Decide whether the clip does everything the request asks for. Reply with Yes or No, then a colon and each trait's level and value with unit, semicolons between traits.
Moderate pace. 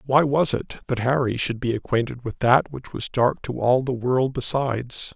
No: fast, 210 wpm